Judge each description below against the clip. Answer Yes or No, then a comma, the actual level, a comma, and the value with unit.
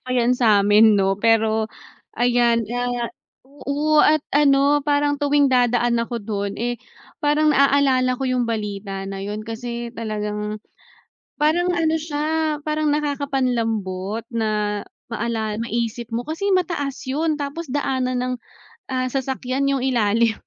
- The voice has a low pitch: No, high, 245 Hz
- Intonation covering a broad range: No, average, 4.4 semitones